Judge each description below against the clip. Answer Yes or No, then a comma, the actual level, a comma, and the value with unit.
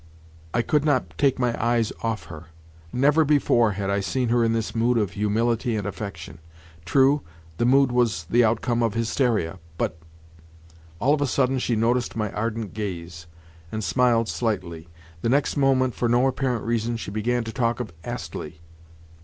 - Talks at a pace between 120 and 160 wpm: No, average, 170 wpm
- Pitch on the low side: Yes, low, 115 Hz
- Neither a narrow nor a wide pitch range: Yes, average, 3.0 semitones